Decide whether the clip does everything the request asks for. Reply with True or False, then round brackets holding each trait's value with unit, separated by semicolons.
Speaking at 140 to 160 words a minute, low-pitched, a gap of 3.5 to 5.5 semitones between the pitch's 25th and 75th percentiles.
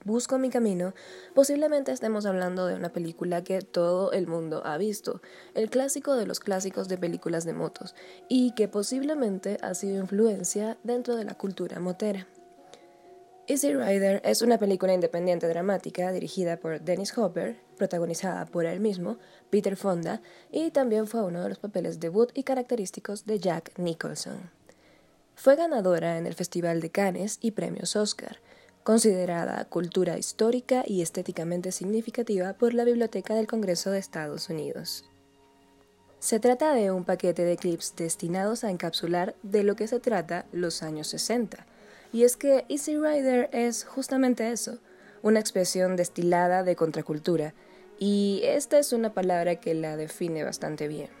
False (150 wpm; 195 Hz; 4.7 semitones)